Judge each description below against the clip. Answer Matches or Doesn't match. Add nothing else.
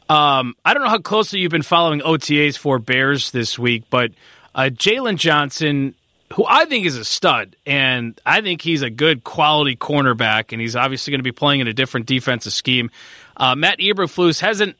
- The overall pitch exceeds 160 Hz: Doesn't match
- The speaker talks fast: Doesn't match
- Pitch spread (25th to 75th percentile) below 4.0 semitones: Doesn't match